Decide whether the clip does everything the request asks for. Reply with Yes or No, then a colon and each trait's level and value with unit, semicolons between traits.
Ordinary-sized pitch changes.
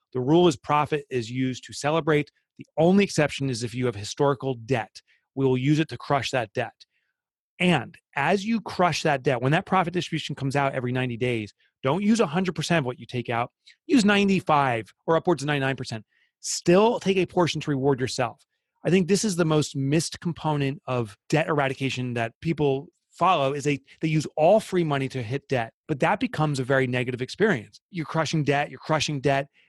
Yes: average, 4.5 semitones